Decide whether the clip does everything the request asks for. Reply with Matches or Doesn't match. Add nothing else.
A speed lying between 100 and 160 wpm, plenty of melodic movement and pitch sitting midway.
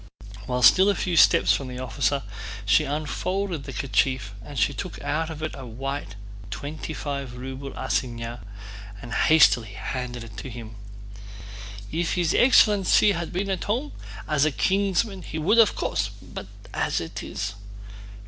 Matches